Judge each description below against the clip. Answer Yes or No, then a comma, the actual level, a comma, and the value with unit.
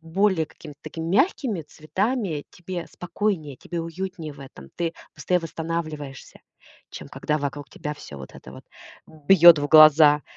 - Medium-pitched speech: Yes, medium, 160 Hz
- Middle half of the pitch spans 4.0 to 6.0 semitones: No, average, 3.3 semitones